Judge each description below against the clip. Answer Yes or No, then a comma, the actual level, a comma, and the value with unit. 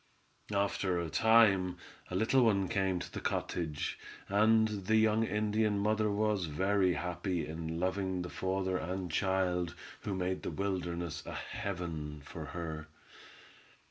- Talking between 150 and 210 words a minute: No, average, 140 wpm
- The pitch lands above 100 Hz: No, very low, 95 Hz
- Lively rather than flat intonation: No, average, 3.0 semitones